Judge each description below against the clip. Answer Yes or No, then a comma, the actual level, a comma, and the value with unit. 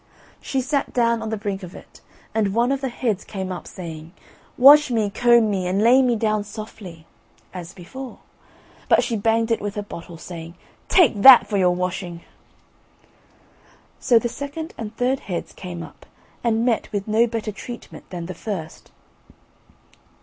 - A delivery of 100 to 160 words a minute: No, average, 170 wpm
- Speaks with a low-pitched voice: No, high, 215 Hz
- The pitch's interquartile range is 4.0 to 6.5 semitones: Yes, average, 4.5 semitones